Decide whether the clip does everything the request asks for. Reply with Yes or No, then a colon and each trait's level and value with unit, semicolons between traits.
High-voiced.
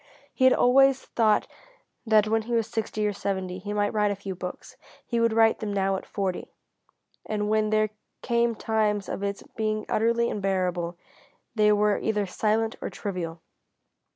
Yes: high, 210 Hz